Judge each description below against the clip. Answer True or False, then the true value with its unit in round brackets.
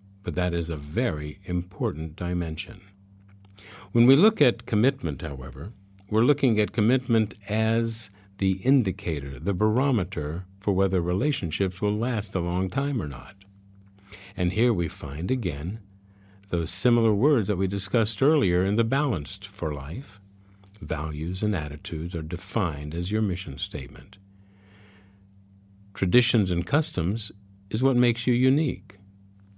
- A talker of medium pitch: False (100 Hz)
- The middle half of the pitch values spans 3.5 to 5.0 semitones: True (3.9 semitones)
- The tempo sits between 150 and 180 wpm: False (135 wpm)